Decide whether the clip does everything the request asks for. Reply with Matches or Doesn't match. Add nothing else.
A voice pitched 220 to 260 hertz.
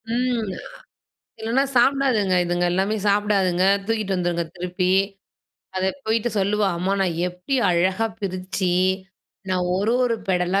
Doesn't match